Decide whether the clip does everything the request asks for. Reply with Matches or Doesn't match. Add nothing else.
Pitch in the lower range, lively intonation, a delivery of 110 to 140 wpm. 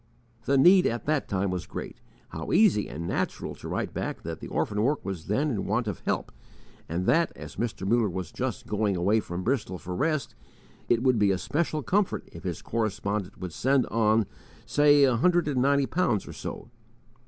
Doesn't match